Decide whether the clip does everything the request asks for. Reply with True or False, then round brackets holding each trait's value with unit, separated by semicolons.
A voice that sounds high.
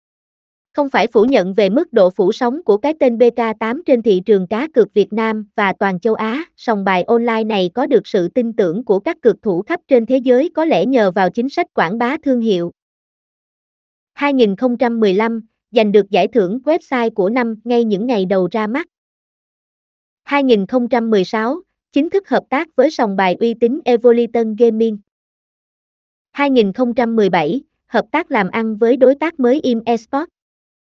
True (240 Hz)